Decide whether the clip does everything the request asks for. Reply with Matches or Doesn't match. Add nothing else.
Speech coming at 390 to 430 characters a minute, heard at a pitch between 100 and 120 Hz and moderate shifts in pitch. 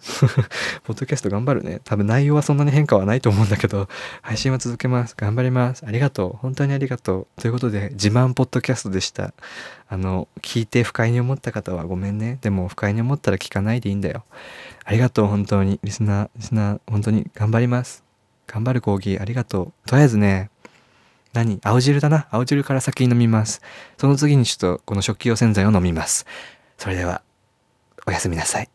Matches